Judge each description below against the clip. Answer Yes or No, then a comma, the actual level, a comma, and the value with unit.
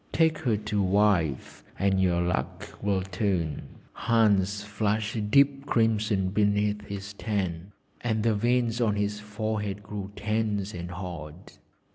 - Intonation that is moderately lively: No, narrow, 2.2 semitones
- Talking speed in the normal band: No, slow, 130 wpm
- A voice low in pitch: Yes, low, 105 Hz